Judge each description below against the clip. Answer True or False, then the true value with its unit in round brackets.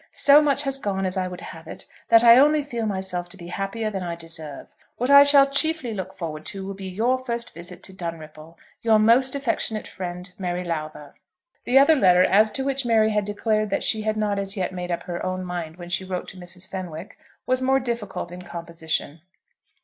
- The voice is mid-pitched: False (195 Hz)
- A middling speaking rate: False (215 wpm)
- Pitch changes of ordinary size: True (4.9 semitones)